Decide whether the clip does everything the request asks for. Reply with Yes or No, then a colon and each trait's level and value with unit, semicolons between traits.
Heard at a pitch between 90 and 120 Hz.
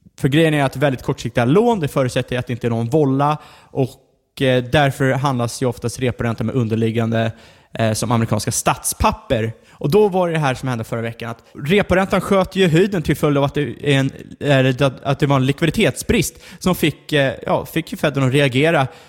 No: low, 135 Hz